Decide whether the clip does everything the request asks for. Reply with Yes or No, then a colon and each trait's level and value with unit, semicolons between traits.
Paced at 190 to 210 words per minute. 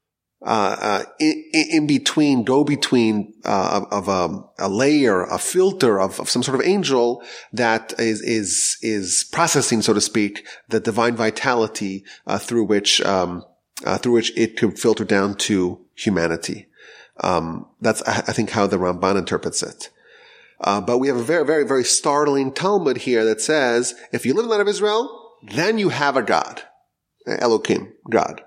No: average, 175 wpm